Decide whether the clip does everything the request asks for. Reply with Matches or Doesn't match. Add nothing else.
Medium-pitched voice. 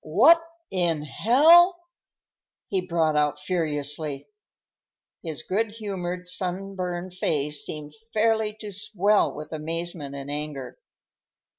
Matches